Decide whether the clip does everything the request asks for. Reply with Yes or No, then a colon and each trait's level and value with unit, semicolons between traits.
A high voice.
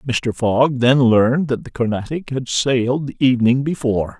No: low, 125 Hz